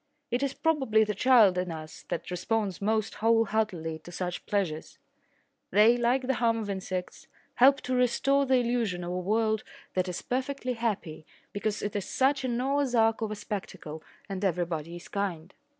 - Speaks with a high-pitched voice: Yes, high, 215 Hz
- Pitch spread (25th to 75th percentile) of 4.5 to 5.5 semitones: Yes, average, 5.2 semitones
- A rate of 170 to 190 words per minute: Yes, average, 175 wpm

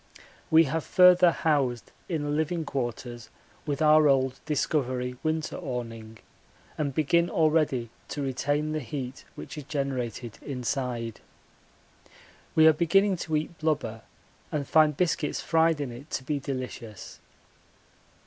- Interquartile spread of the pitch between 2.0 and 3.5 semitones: No, average, 3.9 semitones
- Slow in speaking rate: Yes, slow, 130 wpm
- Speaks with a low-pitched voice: No, medium, 145 Hz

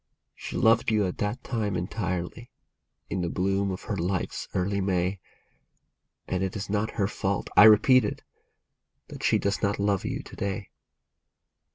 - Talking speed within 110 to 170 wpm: Yes, average, 165 wpm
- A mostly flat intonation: Yes, narrow, 2.1 semitones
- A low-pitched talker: Yes, low, 100 Hz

